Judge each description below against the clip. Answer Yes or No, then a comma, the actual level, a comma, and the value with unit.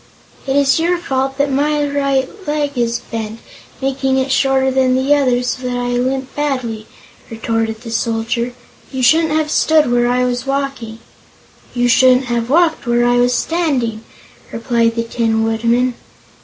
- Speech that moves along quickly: No, average, 160 wpm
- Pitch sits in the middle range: No, very high, 255 Hz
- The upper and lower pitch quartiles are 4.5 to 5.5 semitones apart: No, average, 2.7 semitones